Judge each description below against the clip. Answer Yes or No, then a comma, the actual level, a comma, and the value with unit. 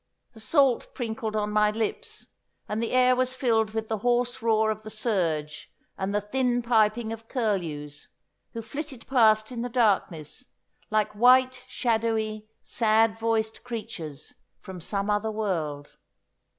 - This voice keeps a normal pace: Yes, average, 145 wpm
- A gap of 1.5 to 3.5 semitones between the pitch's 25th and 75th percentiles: Yes, narrow, 2.4 semitones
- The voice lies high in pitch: Yes, high, 220 Hz